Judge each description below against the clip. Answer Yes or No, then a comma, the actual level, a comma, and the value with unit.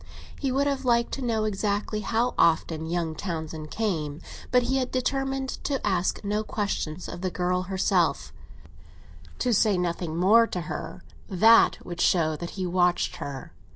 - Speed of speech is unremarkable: Yes, average, 155 wpm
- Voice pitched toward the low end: No, high, 195 Hz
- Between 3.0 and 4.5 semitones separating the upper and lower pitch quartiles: No, average, 5.3 semitones